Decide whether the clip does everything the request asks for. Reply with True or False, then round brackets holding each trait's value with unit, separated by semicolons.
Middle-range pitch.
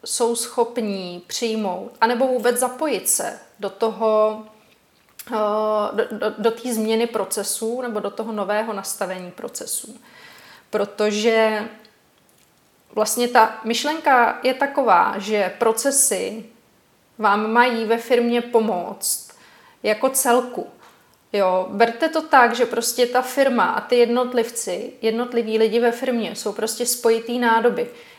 False (230 Hz)